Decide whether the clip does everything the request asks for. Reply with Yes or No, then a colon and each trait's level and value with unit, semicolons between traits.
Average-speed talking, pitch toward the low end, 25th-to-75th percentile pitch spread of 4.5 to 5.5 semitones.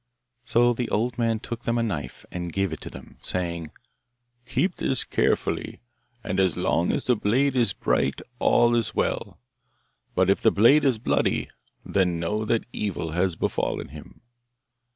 Yes: average, 165 wpm; low, 110 Hz; average, 5.0 semitones